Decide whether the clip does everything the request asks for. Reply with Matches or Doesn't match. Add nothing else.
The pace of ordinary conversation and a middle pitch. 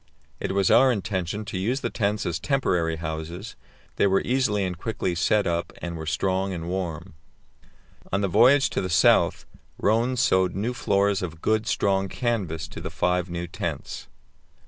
Doesn't match